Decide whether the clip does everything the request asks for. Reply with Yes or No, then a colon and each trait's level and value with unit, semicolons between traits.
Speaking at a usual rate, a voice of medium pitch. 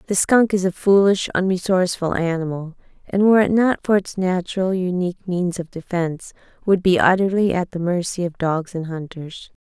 Yes: average, 175 wpm; medium, 180 Hz